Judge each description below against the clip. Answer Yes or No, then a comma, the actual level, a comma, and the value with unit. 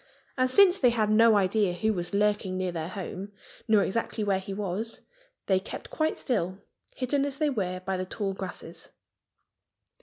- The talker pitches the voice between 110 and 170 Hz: No, high, 205 Hz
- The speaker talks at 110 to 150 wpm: No, average, 175 wpm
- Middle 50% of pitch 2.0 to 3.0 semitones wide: No, average, 3.6 semitones